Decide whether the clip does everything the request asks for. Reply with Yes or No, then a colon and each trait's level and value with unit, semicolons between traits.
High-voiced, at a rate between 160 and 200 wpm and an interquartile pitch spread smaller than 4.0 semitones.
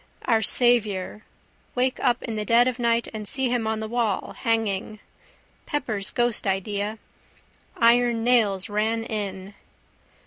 No: high, 225 Hz; slow, 135 wpm; narrow, 2.5 semitones